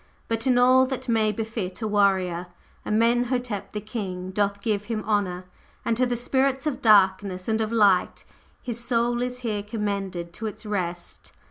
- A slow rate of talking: No, average, 165 wpm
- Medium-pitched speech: No, high, 215 Hz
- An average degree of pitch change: Yes, average, 3.3 semitones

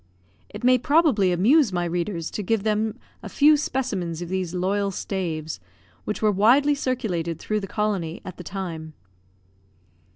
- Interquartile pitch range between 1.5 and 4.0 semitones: No, average, 4.4 semitones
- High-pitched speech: Yes, high, 195 Hz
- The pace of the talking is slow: No, average, 155 wpm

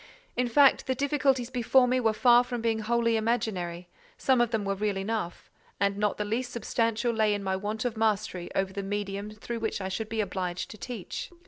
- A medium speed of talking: No, fast, 210 wpm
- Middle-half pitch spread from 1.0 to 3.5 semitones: Yes, average, 3.1 semitones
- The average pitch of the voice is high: Yes, high, 220 Hz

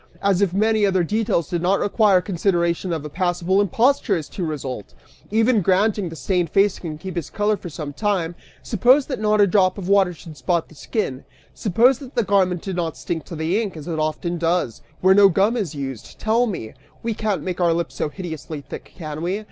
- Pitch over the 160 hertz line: Yes, medium, 185 Hz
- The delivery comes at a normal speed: No, fast, 220 wpm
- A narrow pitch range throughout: No, average, 3.9 semitones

